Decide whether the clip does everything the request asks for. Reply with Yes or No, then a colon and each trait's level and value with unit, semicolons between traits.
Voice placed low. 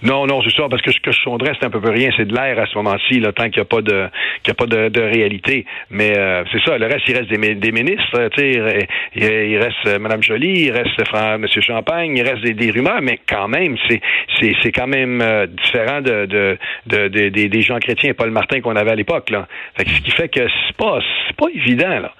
Yes: low, 115 Hz